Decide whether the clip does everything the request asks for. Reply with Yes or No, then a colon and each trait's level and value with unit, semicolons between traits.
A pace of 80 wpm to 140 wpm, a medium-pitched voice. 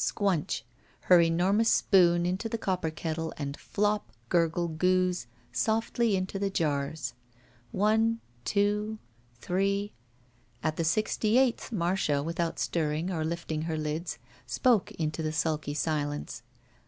Yes: slow, 135 wpm; medium, 170 Hz